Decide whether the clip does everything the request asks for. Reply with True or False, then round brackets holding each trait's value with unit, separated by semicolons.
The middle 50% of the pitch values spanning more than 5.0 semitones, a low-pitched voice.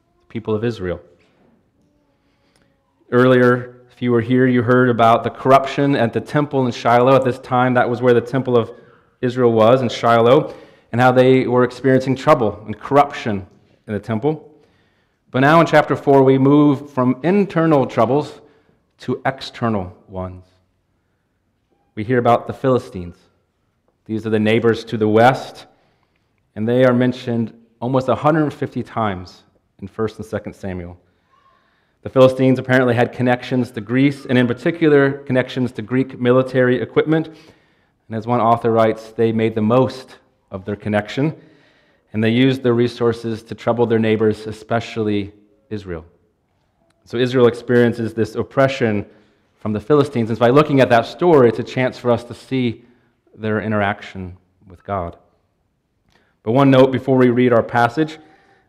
False (3.2 semitones; 120 Hz)